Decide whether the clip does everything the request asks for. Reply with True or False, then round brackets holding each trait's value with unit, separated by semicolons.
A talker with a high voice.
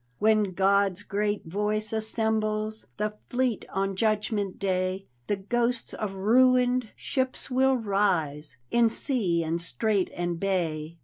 True (210 Hz)